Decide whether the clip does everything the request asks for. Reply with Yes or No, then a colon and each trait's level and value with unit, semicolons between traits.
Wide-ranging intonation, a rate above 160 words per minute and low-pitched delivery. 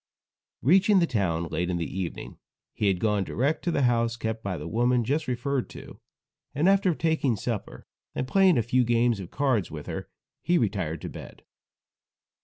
Yes: wide, 6.5 semitones; average, 185 wpm; low, 120 Hz